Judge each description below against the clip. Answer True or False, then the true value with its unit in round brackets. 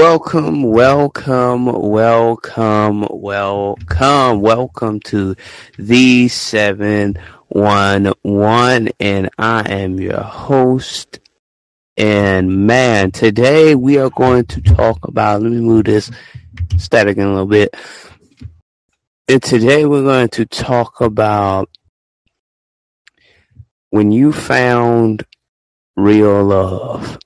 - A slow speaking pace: True (90 wpm)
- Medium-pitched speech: False (105 Hz)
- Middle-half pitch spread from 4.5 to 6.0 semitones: False (3.8 semitones)